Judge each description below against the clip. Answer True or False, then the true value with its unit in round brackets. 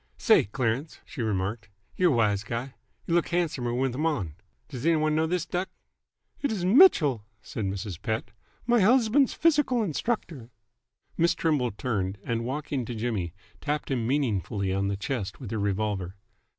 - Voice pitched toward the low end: True (125 Hz)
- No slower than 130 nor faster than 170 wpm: True (165 wpm)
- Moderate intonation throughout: False (7.7 semitones)